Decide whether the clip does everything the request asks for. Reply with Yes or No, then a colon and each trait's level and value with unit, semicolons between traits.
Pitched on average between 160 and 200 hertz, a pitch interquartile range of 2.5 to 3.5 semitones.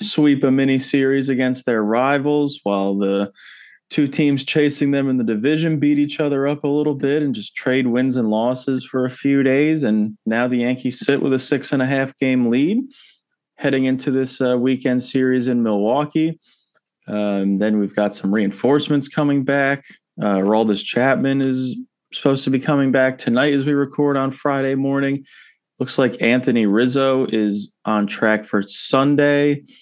No: low, 135 Hz; average, 2.9 semitones